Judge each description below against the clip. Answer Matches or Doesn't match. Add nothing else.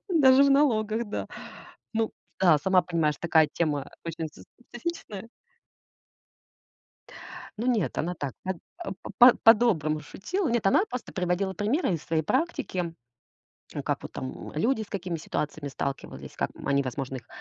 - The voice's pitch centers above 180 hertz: Matches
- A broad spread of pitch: Matches